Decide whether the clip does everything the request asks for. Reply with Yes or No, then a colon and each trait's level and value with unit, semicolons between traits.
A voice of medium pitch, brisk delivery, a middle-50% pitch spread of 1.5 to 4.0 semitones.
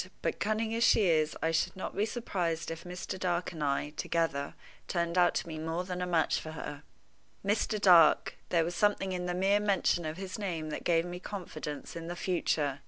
Yes: medium, 175 Hz; fast, 210 wpm; average, 2.8 semitones